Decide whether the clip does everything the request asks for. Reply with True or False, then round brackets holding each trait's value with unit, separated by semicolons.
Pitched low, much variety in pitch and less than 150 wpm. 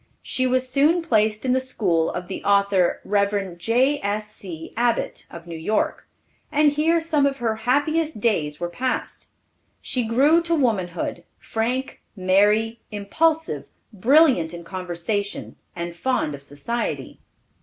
False (220 Hz; 6.2 semitones; 135 wpm)